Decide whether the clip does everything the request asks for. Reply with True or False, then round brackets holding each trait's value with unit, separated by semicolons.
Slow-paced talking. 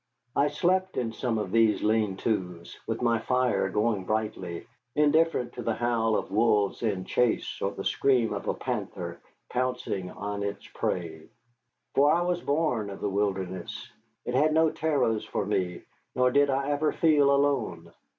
False (165 wpm)